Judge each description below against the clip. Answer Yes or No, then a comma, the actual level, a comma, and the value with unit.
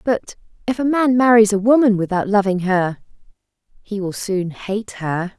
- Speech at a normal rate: Yes, average, 165 wpm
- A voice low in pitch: No, high, 210 Hz